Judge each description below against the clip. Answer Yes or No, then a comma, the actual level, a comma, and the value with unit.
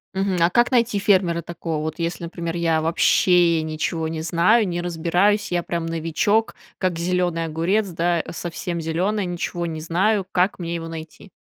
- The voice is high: No, medium, 170 Hz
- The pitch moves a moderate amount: No, narrow, 2.1 semitones